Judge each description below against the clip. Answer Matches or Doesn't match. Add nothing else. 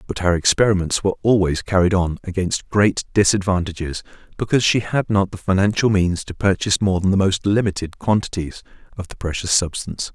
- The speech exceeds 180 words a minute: Doesn't match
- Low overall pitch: Matches